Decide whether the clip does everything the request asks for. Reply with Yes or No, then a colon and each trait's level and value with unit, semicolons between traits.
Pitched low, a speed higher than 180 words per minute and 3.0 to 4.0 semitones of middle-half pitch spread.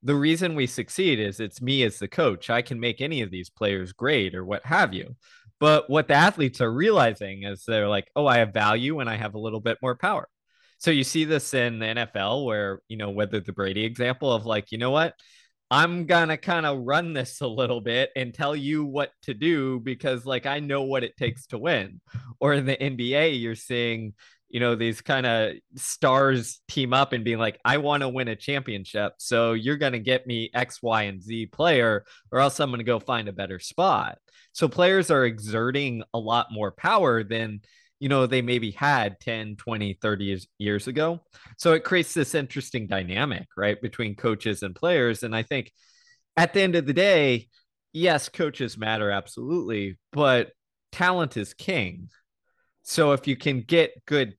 No: low, 125 Hz; fast, 205 wpm; average, 4.7 semitones